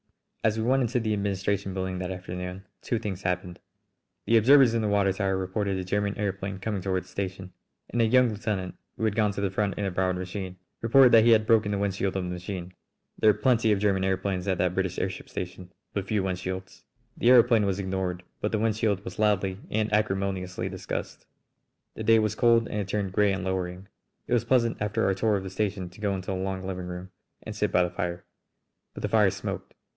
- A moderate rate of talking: No, fast, 230 wpm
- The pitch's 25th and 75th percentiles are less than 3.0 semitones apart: Yes, narrow, 2.5 semitones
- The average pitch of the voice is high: No, low, 100 Hz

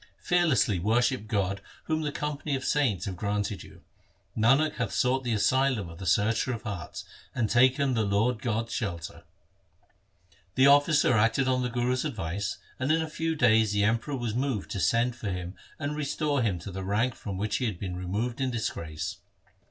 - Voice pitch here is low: Yes, low, 115 Hz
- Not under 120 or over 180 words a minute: No, average, 190 wpm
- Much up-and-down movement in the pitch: No, average, 4.6 semitones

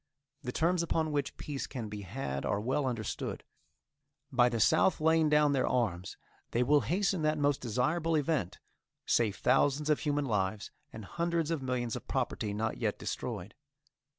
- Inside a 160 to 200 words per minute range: Yes, average, 165 wpm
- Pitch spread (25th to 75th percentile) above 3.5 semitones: Yes, wide, 5.4 semitones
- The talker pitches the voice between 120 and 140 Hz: Yes, low, 135 Hz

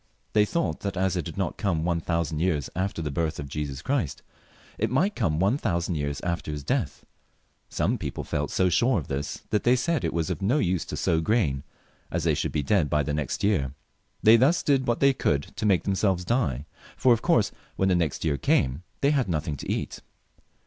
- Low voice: Yes, very low, 90 Hz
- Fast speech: Yes, fast, 220 wpm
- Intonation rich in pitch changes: Yes, wide, 6.4 semitones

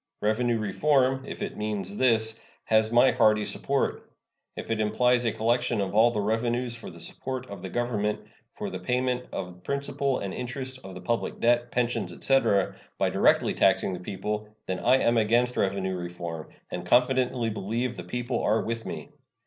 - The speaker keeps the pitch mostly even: No, average, 3.0 semitones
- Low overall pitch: Yes, low, 115 Hz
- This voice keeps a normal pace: Yes, average, 175 wpm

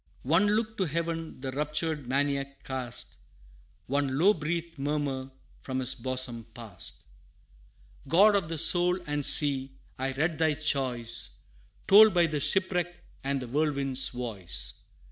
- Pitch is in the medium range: Yes, medium, 145 Hz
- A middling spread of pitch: Yes, average, 4.0 semitones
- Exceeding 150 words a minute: No, slow, 135 wpm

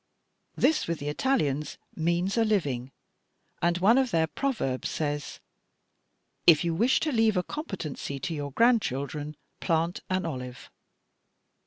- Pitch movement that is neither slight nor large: No, wide, 7.0 semitones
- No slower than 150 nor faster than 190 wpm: No, slow, 135 wpm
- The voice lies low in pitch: No, medium, 170 Hz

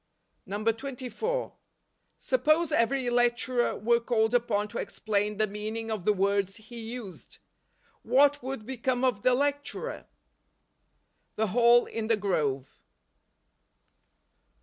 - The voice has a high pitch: Yes, high, 230 Hz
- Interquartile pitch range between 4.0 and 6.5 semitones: No, average, 3.4 semitones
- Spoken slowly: Yes, slow, 115 wpm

